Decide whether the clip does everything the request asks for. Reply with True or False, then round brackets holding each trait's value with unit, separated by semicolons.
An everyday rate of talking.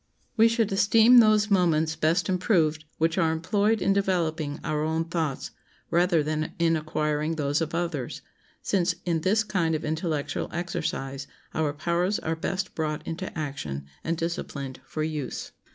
True (150 wpm)